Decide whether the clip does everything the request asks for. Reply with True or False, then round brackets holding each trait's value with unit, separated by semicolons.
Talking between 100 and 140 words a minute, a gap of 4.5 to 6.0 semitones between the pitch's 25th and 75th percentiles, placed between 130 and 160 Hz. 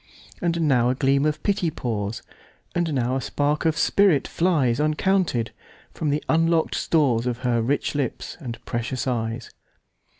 True (135 wpm; 5.0 semitones; 140 Hz)